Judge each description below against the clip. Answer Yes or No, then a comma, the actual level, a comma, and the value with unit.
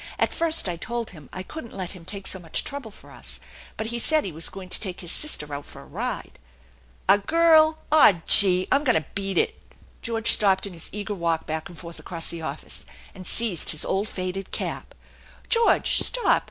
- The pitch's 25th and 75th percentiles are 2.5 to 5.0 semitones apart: No, wide, 5.5 semitones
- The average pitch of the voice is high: Yes, high, 195 Hz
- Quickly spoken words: Yes, fast, 220 wpm